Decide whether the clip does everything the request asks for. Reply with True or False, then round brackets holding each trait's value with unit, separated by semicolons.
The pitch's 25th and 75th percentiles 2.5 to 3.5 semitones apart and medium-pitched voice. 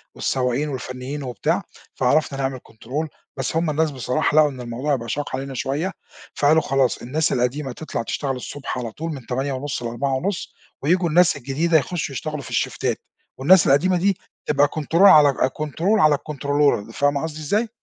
True (3.0 semitones; 145 Hz)